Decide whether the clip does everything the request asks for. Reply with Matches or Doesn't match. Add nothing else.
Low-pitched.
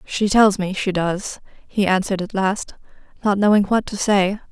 Doesn't match